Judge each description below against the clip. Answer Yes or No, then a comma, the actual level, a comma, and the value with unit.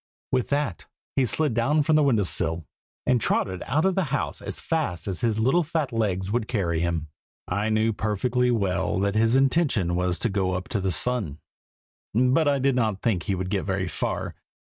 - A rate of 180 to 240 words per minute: Yes, average, 200 wpm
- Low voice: Yes, low, 110 Hz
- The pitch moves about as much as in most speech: No, wide, 5.8 semitones